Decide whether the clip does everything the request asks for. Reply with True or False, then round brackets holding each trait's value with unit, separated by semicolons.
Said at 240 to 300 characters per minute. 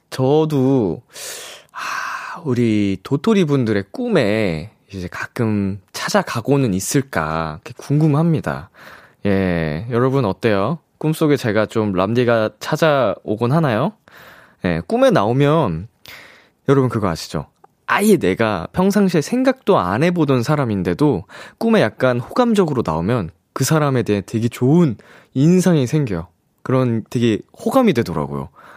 True (265 characters per minute)